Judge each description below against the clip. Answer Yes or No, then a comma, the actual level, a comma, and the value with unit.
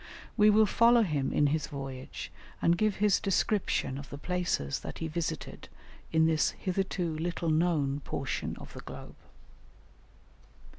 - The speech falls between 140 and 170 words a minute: Yes, average, 145 wpm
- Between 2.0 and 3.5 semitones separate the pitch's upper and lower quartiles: No, average, 4.8 semitones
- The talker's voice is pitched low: No, medium, 165 Hz